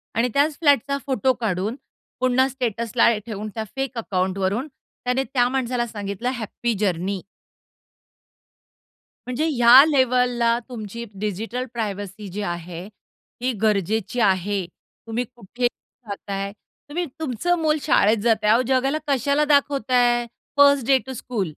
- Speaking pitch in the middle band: No, high, 240 Hz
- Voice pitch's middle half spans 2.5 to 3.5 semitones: No, average, 4.1 semitones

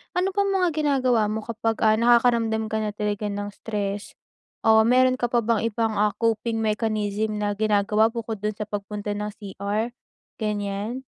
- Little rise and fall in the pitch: Yes, narrow, 2.0 semitones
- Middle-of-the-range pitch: No, high, 220 Hz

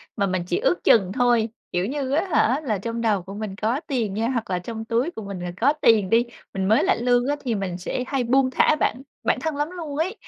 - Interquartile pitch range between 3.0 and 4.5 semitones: No, average, 5.2 semitones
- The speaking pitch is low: No, high, 230 Hz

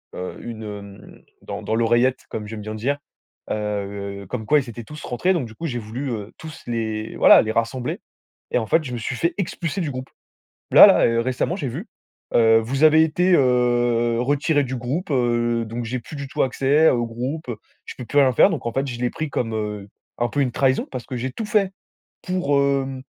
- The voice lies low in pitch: Yes, low, 125 Hz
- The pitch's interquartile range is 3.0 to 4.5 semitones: Yes, average, 3.8 semitones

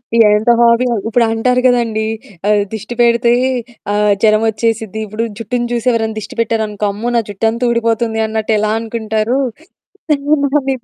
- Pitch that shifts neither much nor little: No, narrow, 1.7 semitones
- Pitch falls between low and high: No, high, 225 Hz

